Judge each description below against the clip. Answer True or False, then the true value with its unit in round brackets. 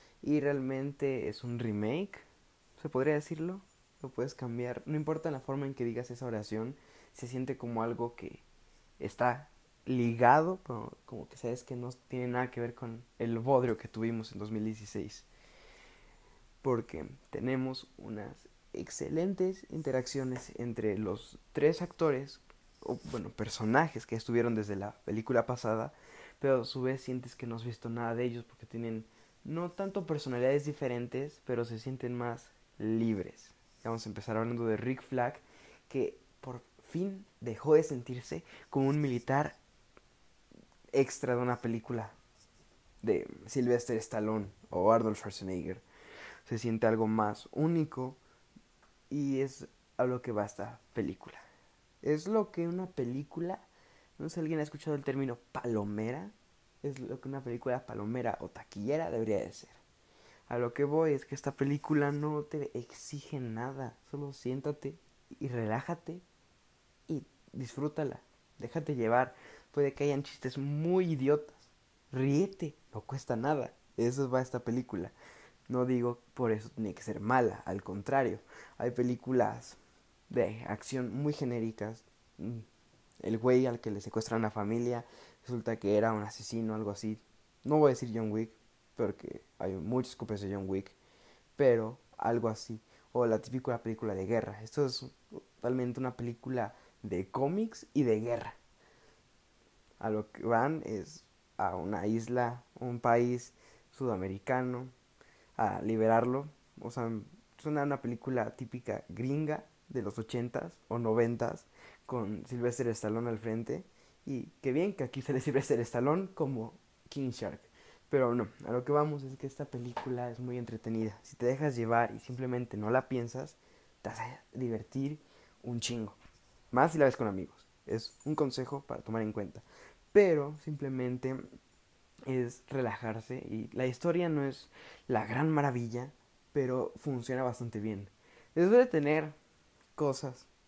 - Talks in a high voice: False (125 Hz)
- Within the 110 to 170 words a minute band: True (150 wpm)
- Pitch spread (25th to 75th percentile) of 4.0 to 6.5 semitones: False (3.4 semitones)